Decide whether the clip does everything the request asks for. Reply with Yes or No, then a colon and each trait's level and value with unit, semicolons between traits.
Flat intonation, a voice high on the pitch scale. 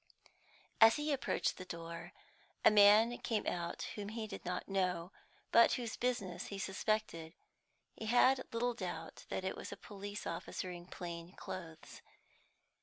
No: average, 4.2 semitones; high, 200 Hz